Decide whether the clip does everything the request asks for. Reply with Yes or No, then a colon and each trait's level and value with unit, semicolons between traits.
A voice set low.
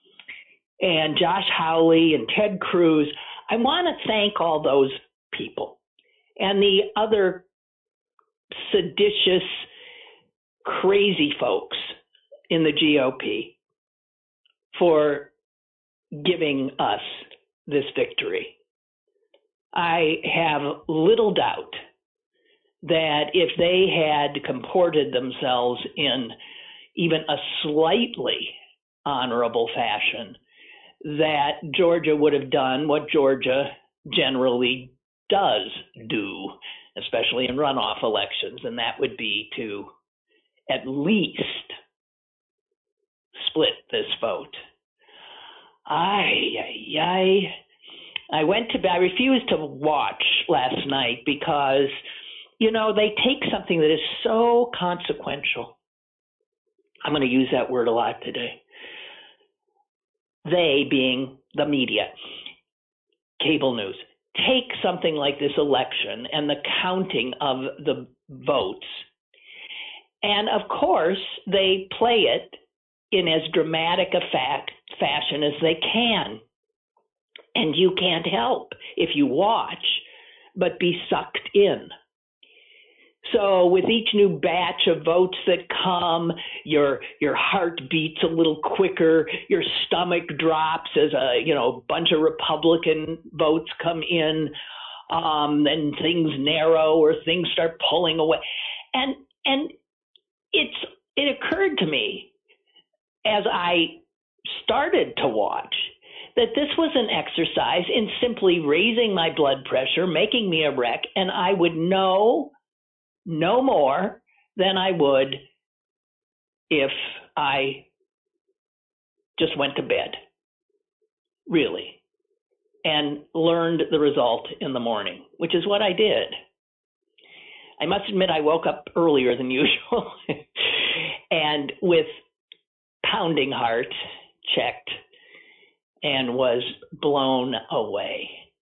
No: high, 190 Hz